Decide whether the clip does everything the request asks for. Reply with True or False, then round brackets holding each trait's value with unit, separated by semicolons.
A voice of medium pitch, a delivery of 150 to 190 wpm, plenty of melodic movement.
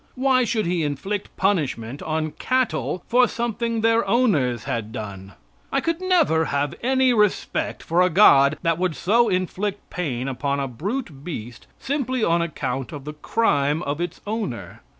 True (175 Hz; 160 wpm; 8.4 semitones)